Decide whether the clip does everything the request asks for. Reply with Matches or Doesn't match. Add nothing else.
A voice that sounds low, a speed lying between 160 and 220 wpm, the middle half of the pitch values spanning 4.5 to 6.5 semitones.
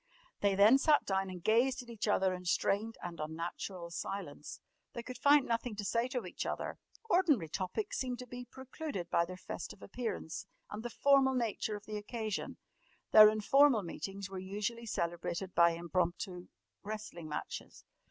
Doesn't match